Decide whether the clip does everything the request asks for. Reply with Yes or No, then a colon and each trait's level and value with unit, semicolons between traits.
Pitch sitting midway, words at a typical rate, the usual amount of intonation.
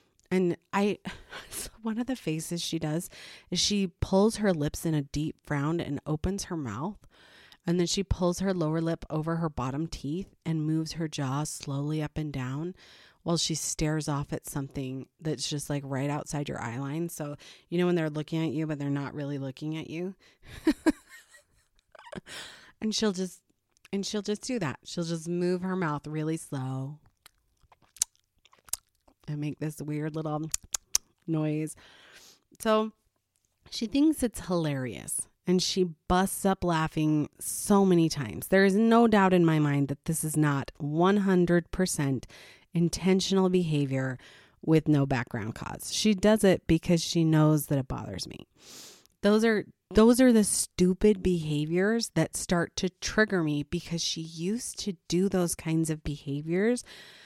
Yes: medium, 165 Hz; average, 160 wpm; average, 4.0 semitones